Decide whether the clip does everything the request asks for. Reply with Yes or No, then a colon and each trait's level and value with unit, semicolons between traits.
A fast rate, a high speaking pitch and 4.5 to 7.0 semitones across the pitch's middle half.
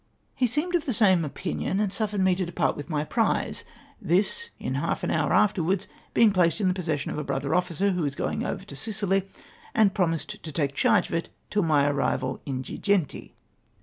No: fast, 210 wpm; medium, 180 Hz; average, 5.2 semitones